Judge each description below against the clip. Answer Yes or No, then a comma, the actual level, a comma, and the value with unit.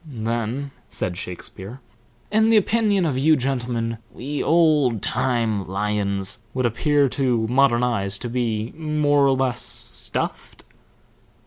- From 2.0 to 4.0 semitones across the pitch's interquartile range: No, average, 4.5 semitones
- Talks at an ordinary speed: No, slow, 125 wpm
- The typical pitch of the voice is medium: No, low, 125 Hz